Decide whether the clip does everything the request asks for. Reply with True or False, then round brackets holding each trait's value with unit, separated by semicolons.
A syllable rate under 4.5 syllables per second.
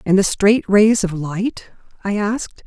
True (4.1 syllables/s)